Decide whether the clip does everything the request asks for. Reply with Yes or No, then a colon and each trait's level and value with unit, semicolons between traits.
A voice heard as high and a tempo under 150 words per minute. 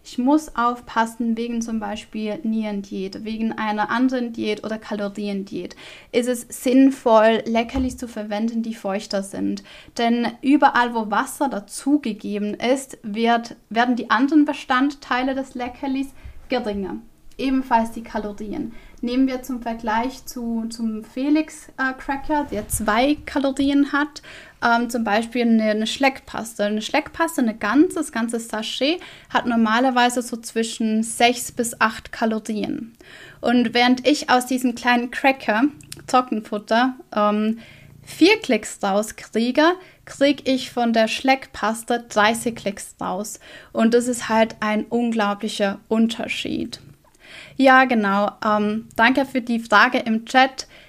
Yes: high, 235 Hz; slow, 125 wpm